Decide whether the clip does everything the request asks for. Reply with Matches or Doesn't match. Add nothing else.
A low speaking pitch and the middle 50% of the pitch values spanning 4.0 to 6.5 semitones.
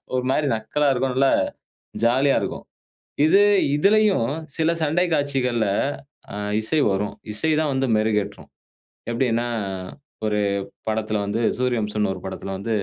Matches